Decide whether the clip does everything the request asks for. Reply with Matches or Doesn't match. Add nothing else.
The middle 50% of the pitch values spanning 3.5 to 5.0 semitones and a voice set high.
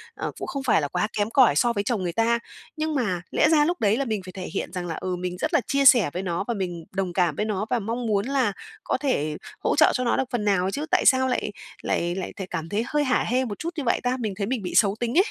Doesn't match